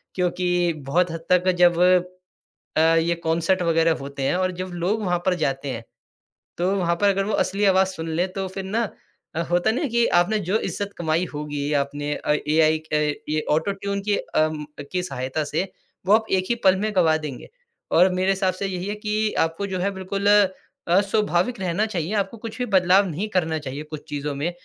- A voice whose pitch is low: No, medium, 180 Hz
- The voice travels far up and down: No, average, 3.6 semitones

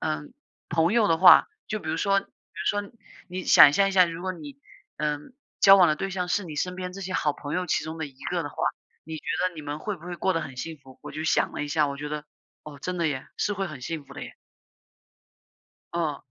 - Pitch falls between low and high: Yes, medium, 165 Hz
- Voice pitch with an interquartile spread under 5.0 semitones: Yes, average, 3.7 semitones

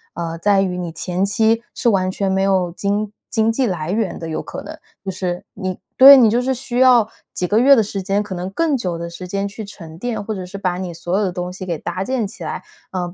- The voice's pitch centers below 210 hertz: Yes, high, 195 Hz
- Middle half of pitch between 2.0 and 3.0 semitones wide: No, average, 3.6 semitones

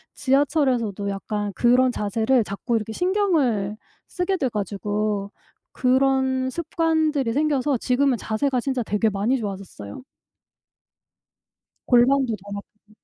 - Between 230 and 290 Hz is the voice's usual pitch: Yes, high, 245 Hz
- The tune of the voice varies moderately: Yes, average, 4.7 semitones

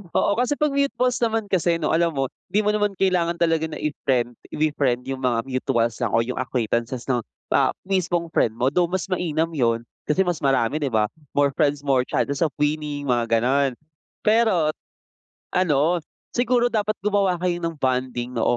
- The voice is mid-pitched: Yes, medium, 155 Hz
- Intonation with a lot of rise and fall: Yes, wide, 6.0 semitones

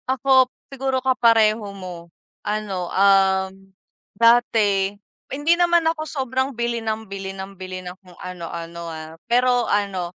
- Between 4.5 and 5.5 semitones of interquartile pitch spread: Yes, average, 5.2 semitones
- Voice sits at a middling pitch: No, high, 205 Hz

